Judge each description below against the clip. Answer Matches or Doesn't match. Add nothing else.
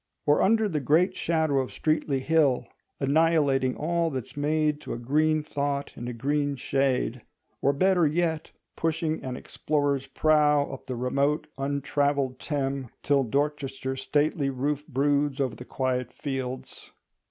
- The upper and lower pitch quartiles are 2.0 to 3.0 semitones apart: Matches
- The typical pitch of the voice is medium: Matches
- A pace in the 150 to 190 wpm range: Doesn't match